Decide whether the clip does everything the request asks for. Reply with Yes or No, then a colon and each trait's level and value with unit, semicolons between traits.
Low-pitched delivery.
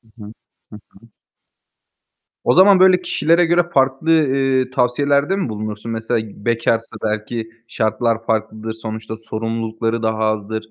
Yes: low, 115 Hz